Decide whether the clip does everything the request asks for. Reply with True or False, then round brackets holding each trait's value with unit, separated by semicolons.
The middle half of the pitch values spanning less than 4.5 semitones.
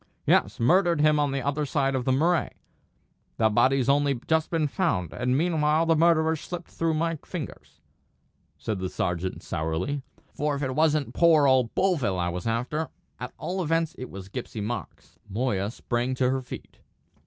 False (5.1 semitones)